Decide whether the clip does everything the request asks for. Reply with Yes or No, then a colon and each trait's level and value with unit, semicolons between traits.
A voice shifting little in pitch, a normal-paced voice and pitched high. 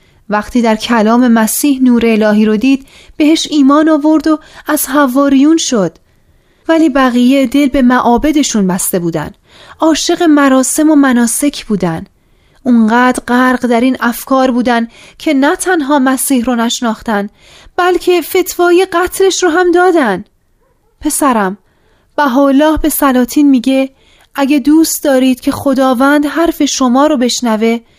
No: average, 4.2 semitones; average, 130 wpm; very high, 270 Hz